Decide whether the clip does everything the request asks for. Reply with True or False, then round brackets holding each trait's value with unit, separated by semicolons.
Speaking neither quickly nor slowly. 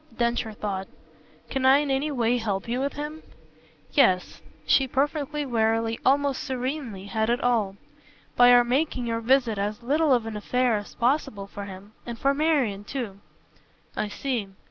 True (165 wpm)